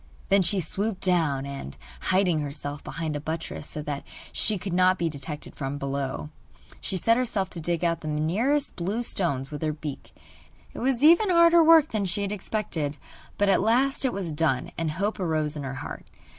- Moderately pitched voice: Yes, medium, 170 Hz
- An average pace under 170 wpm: No, average, 195 wpm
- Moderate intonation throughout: No, wide, 5.7 semitones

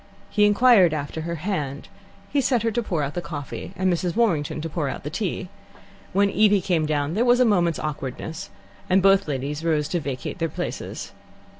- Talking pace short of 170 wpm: No, average, 195 wpm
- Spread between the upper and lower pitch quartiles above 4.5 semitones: Yes, average, 5.0 semitones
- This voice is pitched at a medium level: Yes, medium, 170 Hz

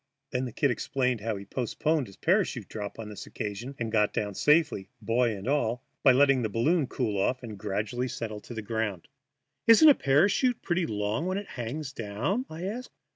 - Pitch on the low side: Yes, low, 120 Hz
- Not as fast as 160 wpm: No, average, 195 wpm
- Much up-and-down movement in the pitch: Yes, wide, 5.7 semitones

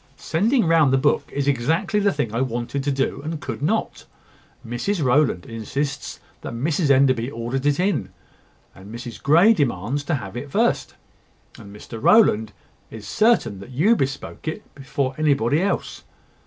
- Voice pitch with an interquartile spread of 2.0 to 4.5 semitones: No, average, 5.1 semitones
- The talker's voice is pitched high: No, medium, 140 Hz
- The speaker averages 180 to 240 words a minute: No, average, 160 wpm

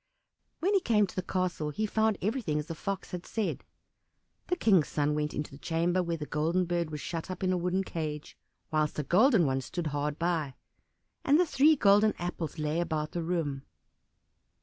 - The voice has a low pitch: No, medium, 170 Hz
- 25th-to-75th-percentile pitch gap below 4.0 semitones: No, average, 4.6 semitones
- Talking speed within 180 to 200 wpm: Yes, average, 195 wpm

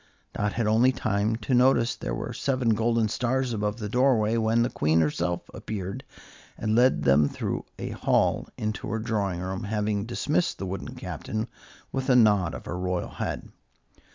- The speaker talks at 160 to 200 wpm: Yes, average, 180 wpm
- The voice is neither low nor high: No, low, 110 Hz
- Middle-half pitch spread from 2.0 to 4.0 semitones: Yes, average, 3.3 semitones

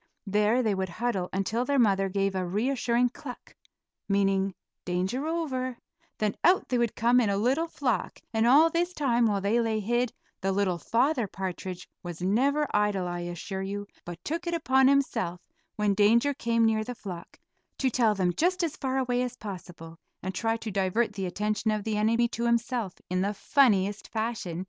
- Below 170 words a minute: No, average, 185 wpm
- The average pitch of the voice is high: Yes, high, 220 Hz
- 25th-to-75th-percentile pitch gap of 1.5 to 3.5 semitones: No, average, 4.3 semitones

